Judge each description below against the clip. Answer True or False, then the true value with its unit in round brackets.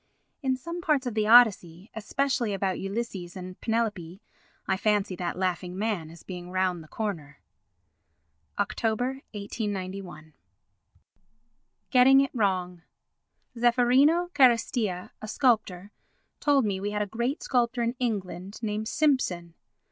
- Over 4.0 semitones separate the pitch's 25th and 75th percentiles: True (4.9 semitones)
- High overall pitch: True (210 Hz)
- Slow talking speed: True (125 wpm)